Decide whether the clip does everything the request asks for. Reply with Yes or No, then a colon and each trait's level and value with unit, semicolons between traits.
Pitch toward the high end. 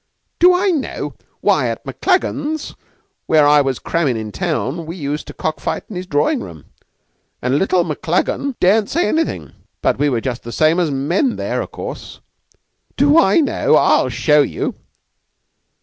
No: medium, 165 Hz